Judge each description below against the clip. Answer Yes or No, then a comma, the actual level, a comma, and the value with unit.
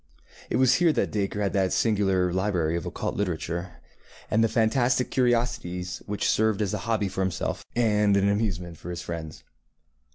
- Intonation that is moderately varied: Yes, average, 3.9 semitones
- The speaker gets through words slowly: No, average, 170 wpm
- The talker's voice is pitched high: No, low, 100 Hz